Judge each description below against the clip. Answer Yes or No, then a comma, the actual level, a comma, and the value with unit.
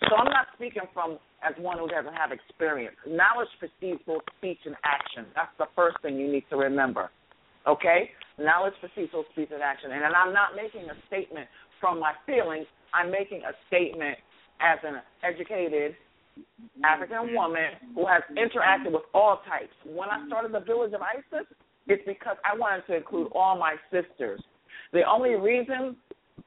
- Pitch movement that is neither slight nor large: No, wide, 5.8 semitones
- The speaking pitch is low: No, medium, 180 Hz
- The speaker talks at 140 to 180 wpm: Yes, average, 170 wpm